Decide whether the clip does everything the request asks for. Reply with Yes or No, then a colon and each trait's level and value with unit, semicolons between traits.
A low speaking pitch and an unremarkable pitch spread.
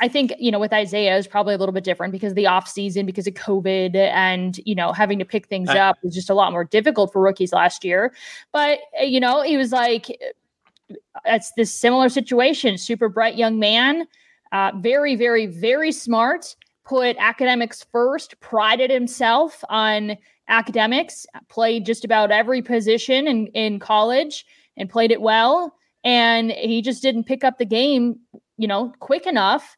No: high, 230 Hz; average, 4.2 semitones